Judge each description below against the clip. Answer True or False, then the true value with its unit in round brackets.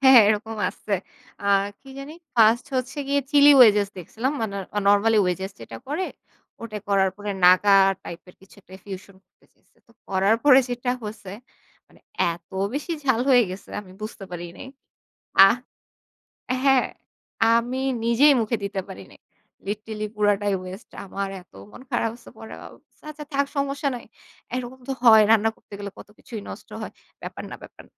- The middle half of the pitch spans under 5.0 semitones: True (4.4 semitones)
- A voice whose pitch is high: True (220 Hz)